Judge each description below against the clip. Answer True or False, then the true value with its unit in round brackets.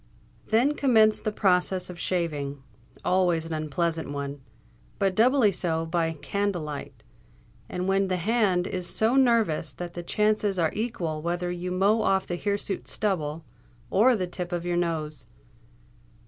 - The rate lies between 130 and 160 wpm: True (145 wpm)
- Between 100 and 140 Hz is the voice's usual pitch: False (180 Hz)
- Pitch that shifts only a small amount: False (3.9 semitones)